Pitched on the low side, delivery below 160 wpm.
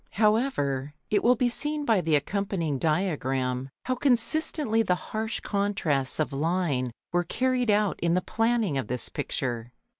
No: medium, 185 Hz; average, 150 wpm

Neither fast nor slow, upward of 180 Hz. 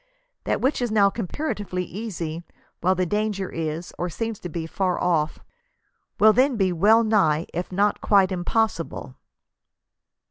Yes: average, 150 wpm; high, 190 Hz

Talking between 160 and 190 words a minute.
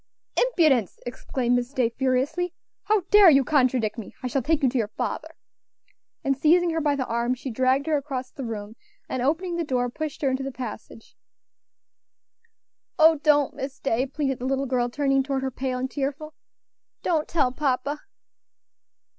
Yes: average, 170 wpm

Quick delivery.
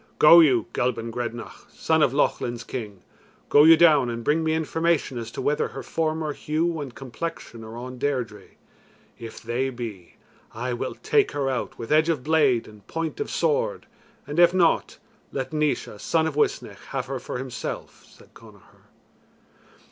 No: average, 170 wpm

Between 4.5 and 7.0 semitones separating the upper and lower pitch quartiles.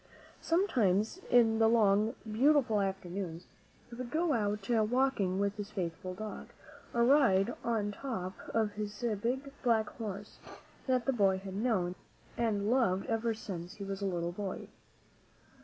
No: average, 3.4 semitones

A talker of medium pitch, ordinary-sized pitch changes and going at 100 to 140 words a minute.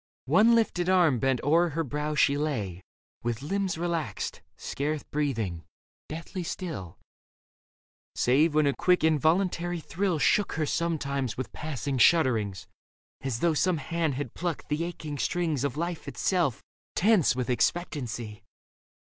Yes: medium, 155 Hz; average, 4.4 semitones; slow, 135 wpm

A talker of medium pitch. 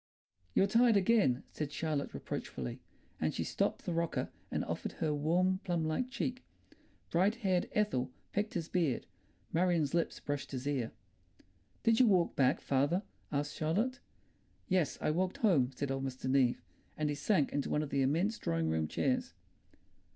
Yes: medium, 160 Hz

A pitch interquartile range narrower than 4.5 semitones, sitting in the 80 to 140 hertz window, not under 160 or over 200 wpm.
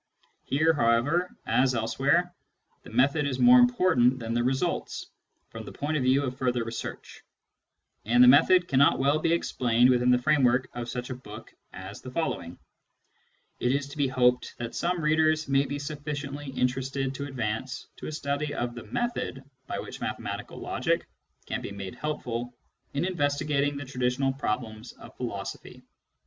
Yes: average, 3.1 semitones; low, 135 Hz; average, 165 wpm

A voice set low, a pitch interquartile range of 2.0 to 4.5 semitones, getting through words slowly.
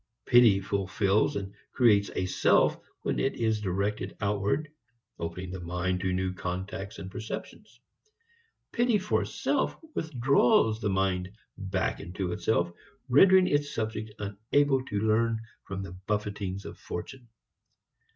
Yes: low, 100 Hz; average, 3.7 semitones; slow, 130 wpm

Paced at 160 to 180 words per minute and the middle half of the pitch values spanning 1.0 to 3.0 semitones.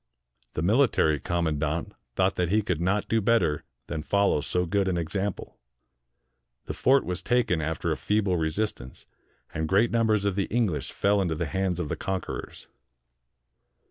No: average, 165 wpm; average, 4.2 semitones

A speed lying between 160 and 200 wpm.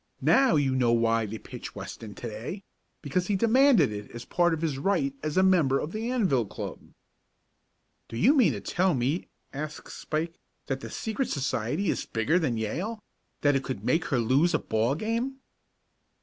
Yes: average, 190 wpm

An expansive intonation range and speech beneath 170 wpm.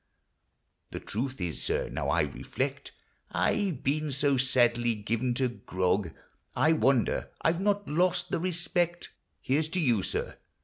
Yes: wide, 5.8 semitones; average, 160 wpm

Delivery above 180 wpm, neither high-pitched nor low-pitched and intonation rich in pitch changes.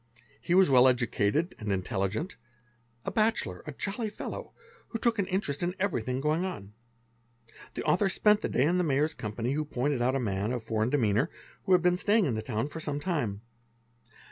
Yes: average, 195 wpm; medium, 145 Hz; wide, 8.1 semitones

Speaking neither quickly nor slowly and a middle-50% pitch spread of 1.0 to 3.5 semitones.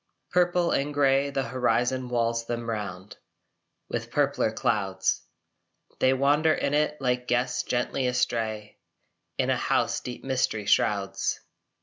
No: slow, 125 wpm; average, 3.0 semitones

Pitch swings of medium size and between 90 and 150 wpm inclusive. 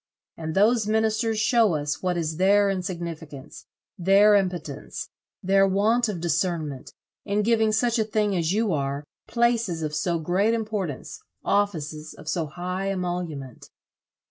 Yes: average, 4.9 semitones; average, 140 wpm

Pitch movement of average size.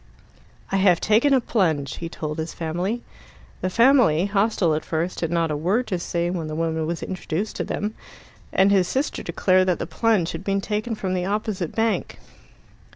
Yes: average, 4.2 semitones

